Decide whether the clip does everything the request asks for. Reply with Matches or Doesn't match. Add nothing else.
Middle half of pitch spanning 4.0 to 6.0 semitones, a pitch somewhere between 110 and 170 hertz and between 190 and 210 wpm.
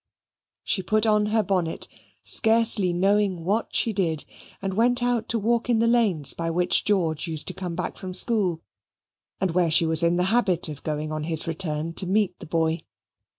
Doesn't match